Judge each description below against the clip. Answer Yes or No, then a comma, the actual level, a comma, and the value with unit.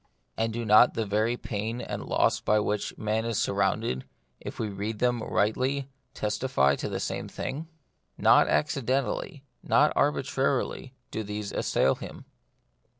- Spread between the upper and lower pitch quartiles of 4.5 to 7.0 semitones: No, average, 3.9 semitones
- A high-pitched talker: No, low, 115 Hz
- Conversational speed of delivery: Yes, average, 150 wpm